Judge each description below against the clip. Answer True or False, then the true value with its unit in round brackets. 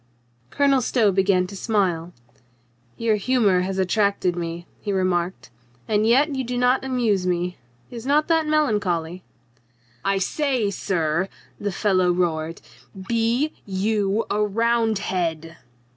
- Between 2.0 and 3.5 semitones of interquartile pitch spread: False (4.5 semitones)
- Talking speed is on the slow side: True (130 wpm)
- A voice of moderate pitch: False (200 Hz)